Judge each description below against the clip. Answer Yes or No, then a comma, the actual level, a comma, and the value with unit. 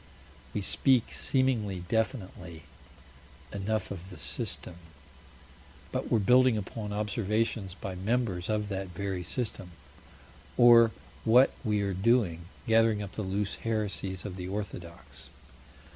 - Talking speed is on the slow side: Yes, slow, 120 wpm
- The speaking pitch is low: Yes, low, 105 Hz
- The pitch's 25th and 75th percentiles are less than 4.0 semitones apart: Yes, average, 3.2 semitones